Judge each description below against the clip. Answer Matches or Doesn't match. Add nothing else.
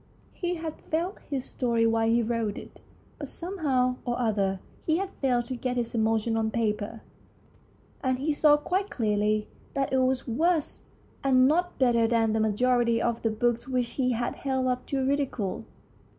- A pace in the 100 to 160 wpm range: Doesn't match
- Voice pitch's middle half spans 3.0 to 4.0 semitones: Matches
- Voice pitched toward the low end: Doesn't match